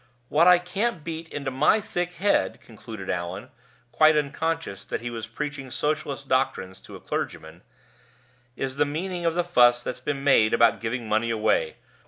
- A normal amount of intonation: No, wide, 6.0 semitones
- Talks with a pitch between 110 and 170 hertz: Yes, medium, 140 Hz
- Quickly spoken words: No, average, 165 wpm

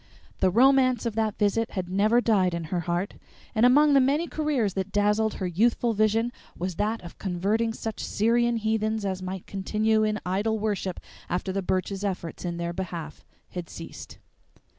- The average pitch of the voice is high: Yes, high, 210 Hz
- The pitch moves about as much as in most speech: Yes, average, 3.3 semitones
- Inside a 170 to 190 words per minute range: Yes, average, 175 wpm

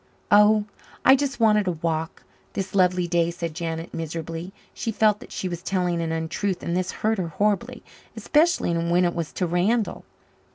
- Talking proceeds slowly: No, average, 175 wpm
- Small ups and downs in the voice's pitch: No, average, 3.9 semitones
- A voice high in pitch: No, medium, 180 Hz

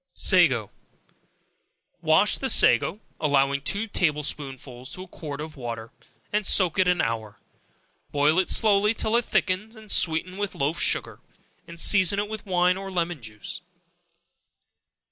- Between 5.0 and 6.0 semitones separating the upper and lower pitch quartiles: Yes, wide, 5.5 semitones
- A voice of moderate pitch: Yes, medium, 170 Hz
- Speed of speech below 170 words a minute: Yes, average, 145 wpm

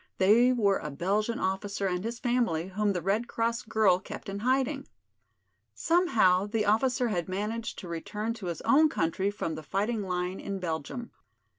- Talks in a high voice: Yes, high, 205 Hz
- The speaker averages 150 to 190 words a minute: Yes, average, 170 wpm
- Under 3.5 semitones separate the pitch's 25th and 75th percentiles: No, average, 4.1 semitones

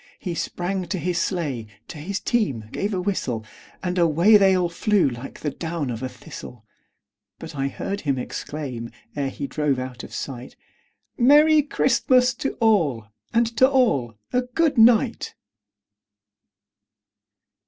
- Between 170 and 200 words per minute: No, average, 145 wpm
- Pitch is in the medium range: Yes, medium, 175 Hz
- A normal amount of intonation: No, wide, 8.7 semitones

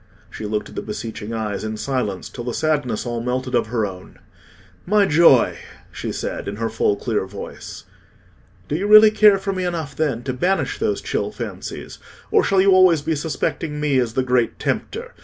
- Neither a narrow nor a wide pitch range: No, wide, 7.0 semitones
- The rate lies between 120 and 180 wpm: No, average, 195 wpm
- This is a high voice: No, low, 130 Hz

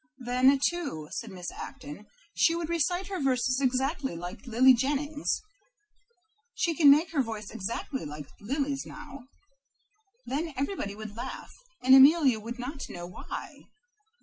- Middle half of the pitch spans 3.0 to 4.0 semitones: No, average, 4.5 semitones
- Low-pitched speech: No, very high, 265 Hz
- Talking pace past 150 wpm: No, average, 140 wpm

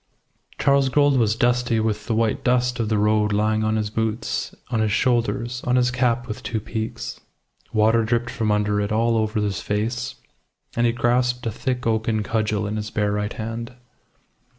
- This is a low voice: Yes, low, 115 Hz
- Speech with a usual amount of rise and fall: No, narrow, 2.3 semitones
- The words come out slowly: No, average, 185 wpm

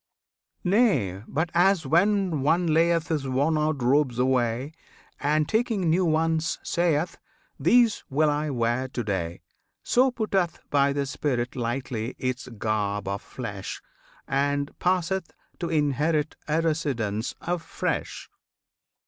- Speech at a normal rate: No, slow, 125 wpm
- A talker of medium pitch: Yes, medium, 150 Hz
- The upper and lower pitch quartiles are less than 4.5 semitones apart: No, average, 4.8 semitones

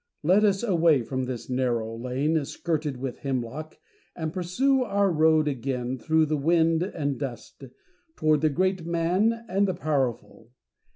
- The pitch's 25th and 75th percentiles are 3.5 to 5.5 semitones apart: Yes, average, 5.2 semitones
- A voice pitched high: No, medium, 155 Hz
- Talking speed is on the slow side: No, average, 150 wpm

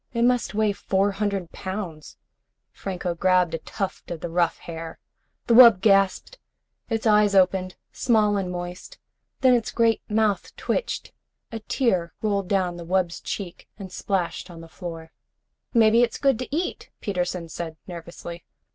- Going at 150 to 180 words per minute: Yes, average, 155 wpm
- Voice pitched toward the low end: No, high, 195 Hz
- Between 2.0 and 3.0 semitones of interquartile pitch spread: No, average, 3.8 semitones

